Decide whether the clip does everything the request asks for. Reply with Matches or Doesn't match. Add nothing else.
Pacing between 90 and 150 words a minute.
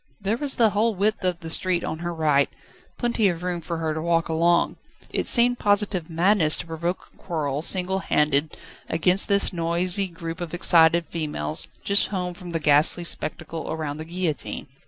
Doesn't match